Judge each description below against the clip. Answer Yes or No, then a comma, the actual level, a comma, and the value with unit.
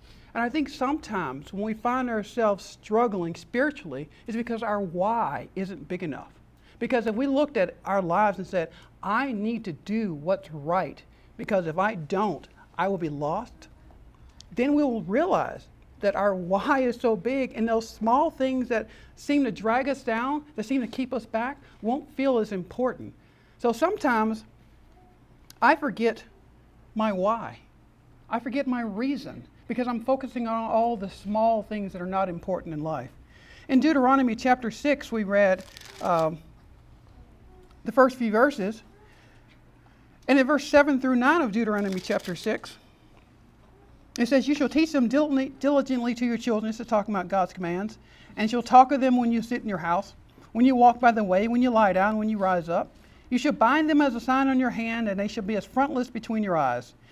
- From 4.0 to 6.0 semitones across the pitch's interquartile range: Yes, average, 4.9 semitones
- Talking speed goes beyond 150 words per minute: Yes, average, 185 wpm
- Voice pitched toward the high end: Yes, high, 225 Hz